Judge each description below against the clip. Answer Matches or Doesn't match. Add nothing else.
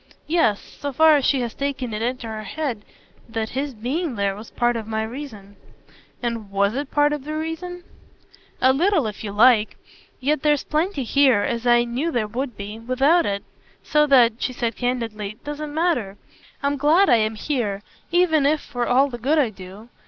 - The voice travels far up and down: Doesn't match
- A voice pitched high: Matches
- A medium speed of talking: Matches